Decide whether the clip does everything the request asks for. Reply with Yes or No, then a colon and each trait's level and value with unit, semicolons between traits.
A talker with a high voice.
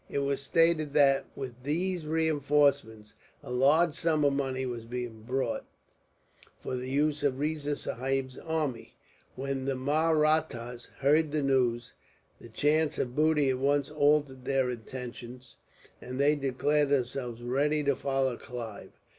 No: medium, 140 Hz